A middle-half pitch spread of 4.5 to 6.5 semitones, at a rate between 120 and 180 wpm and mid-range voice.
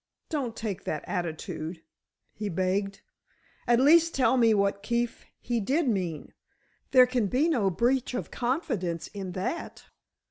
No: average, 5.3 semitones; average, 140 wpm; high, 225 Hz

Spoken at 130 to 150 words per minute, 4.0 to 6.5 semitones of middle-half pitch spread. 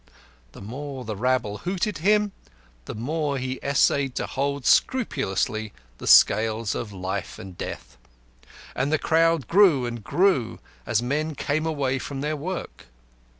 Yes: average, 145 wpm; wide, 5.4 semitones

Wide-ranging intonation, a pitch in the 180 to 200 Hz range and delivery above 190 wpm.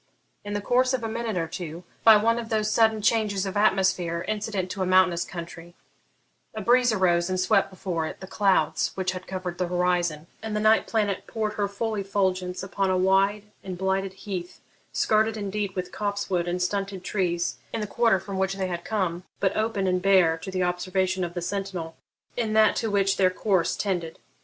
No: narrow, 2.6 semitones; high, 190 Hz; average, 200 wpm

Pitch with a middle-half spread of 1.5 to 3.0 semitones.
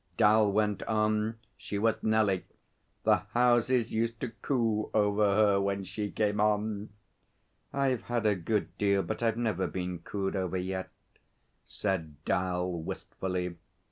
Yes: narrow, 2.6 semitones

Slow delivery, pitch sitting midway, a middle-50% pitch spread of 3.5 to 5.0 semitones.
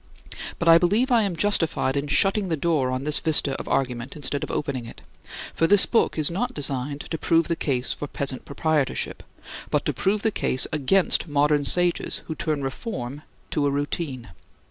No: average, 190 wpm; medium, 150 Hz; average, 3.9 semitones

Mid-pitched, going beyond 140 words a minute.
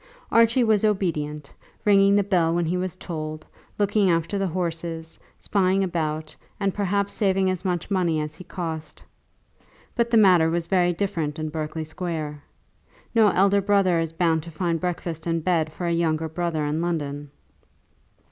Yes: medium, 170 Hz; average, 165 wpm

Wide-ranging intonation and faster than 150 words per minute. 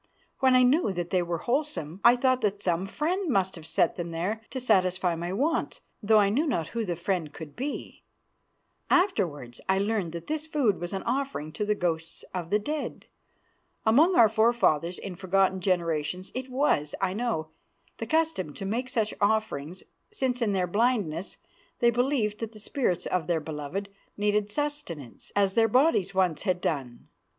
Yes: wide, 6.1 semitones; average, 175 wpm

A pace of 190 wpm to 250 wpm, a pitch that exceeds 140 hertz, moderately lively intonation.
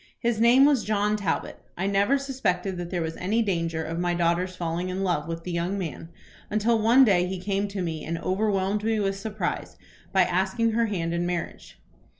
Yes: average, 200 wpm; high, 190 Hz; average, 3.5 semitones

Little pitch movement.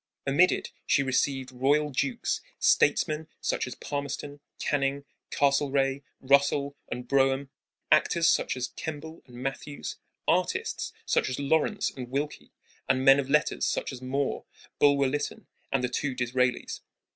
Yes: narrow, 1.8 semitones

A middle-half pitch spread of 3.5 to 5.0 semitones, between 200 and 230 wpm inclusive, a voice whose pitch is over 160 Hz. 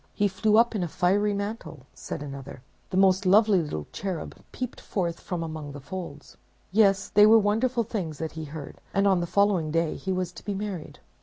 Yes: average, 4.3 semitones; fast, 205 wpm; high, 190 Hz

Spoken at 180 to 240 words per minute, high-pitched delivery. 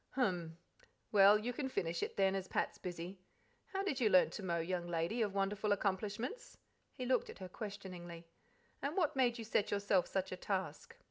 Yes: average, 190 wpm; high, 200 Hz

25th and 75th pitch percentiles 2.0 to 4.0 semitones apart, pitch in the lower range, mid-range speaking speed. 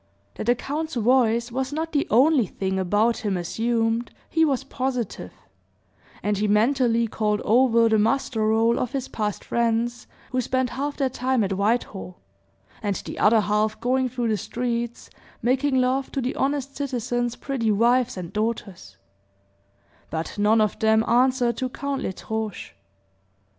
No: average, 3.2 semitones; high, 235 Hz; average, 155 wpm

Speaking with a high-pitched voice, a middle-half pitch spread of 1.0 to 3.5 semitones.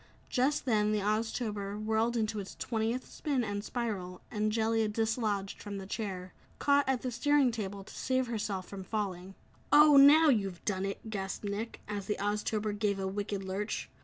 Yes: high, 215 Hz; average, 2.7 semitones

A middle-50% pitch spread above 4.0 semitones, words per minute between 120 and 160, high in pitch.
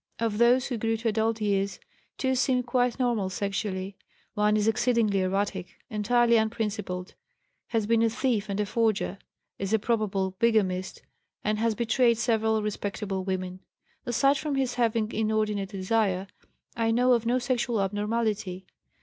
No: average, 2.8 semitones; average, 150 wpm; high, 220 Hz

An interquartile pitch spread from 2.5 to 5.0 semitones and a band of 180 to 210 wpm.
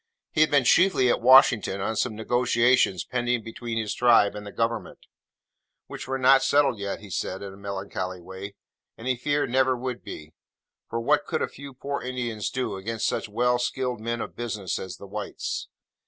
Yes: average, 3.9 semitones; average, 190 wpm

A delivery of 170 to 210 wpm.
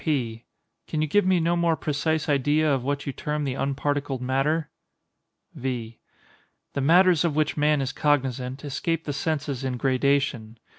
No: average, 160 wpm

